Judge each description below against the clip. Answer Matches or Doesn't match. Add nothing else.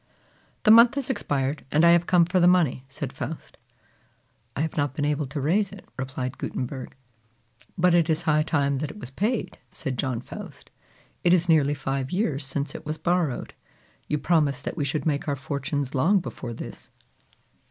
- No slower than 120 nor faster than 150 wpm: Doesn't match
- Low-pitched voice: Doesn't match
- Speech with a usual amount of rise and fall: Matches